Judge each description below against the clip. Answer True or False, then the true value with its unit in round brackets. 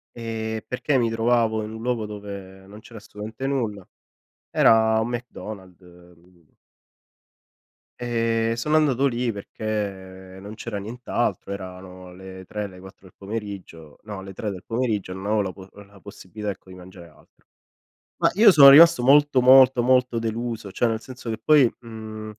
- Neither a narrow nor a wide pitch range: True (3.8 semitones)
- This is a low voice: True (110 Hz)